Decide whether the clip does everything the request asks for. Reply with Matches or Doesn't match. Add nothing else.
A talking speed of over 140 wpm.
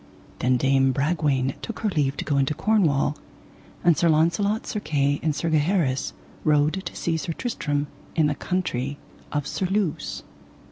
Matches